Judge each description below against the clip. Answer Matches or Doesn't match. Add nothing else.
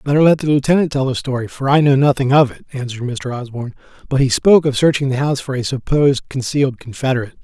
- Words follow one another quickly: Matches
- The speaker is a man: Matches